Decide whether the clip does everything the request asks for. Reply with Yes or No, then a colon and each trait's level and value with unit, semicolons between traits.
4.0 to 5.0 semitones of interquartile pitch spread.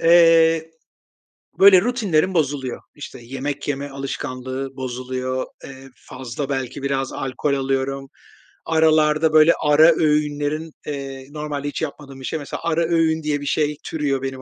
No: average, 2.9 semitones